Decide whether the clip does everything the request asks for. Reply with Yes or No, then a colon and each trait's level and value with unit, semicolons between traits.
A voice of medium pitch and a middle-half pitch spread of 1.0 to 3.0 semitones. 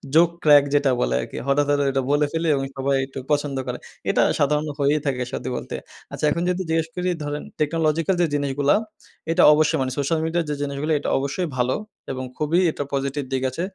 Yes: medium, 145 Hz; average, 2.7 semitones